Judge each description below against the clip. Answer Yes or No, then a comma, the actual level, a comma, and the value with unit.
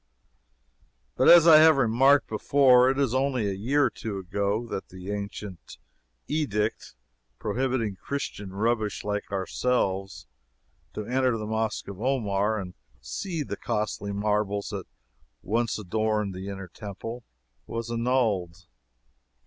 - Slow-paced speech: Yes, slow, 130 wpm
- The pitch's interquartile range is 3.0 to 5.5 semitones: Yes, average, 4.0 semitones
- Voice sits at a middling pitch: No, low, 110 Hz